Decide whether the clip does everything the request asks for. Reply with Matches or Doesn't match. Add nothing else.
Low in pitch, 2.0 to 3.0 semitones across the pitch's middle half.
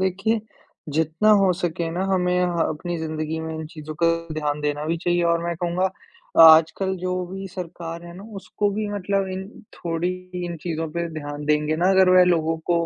Doesn't match